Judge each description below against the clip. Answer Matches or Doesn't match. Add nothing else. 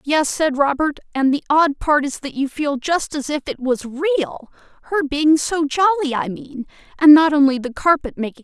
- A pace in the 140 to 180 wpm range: Doesn't match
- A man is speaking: Doesn't match